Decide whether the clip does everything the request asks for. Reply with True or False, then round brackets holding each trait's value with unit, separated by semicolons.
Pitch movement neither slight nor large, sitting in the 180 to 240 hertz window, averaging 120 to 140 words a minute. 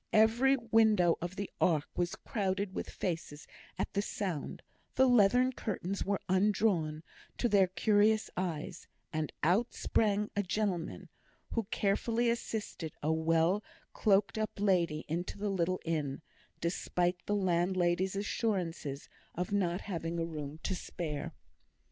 True (3.8 semitones; 190 Hz; 135 wpm)